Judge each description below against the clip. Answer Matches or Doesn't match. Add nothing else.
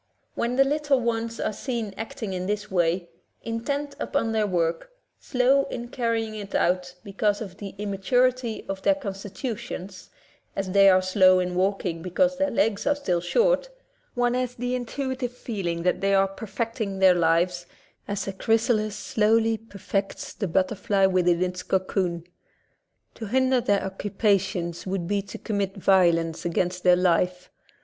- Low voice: Doesn't match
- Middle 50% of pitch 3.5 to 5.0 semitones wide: Matches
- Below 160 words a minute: Doesn't match